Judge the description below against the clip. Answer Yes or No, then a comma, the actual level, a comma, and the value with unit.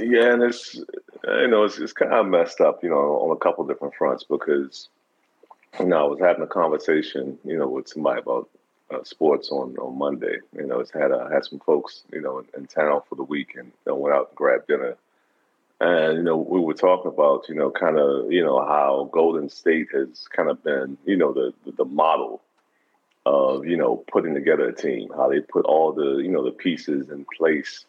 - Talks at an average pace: No, fast, 210 wpm